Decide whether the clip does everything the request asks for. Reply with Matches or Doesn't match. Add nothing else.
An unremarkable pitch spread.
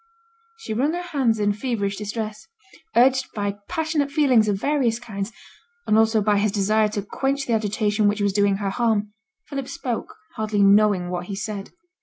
Matches